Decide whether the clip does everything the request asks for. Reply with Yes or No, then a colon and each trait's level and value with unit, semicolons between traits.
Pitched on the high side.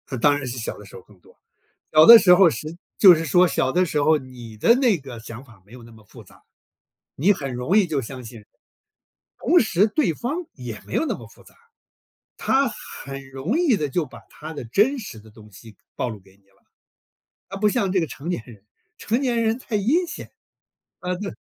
No: medium, 155 Hz